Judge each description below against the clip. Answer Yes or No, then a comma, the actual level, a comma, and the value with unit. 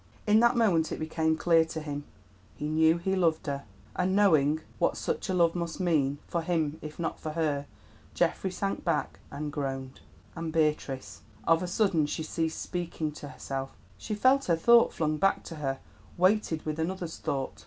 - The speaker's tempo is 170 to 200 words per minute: Yes, average, 185 wpm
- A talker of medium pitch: Yes, medium, 160 Hz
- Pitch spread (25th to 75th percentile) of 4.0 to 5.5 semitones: No, average, 3.1 semitones